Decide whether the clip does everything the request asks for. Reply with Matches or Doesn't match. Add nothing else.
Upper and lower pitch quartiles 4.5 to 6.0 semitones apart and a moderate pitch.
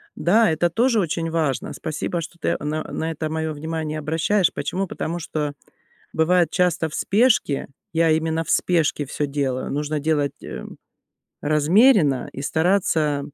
Doesn't match